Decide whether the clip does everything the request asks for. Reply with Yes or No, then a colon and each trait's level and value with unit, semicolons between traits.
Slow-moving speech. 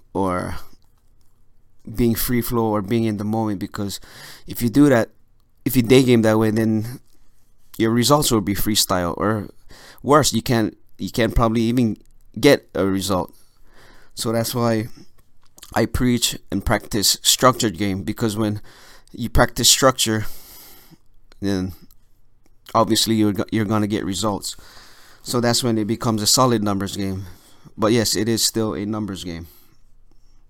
No: average, 150 wpm